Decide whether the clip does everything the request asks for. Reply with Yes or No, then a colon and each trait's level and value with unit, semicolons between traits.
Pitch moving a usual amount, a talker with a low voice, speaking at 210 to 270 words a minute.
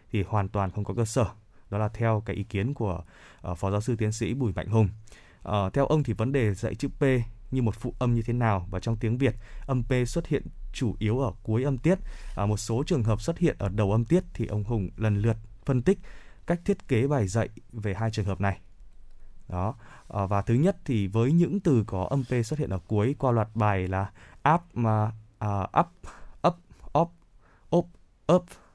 Yes: average, 4.3 semitones; low, 110 Hz; average, 230 wpm